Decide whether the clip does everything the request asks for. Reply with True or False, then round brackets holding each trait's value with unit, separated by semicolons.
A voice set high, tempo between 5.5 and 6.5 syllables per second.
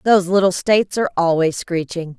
False (180 Hz; 6.0 syllables/s)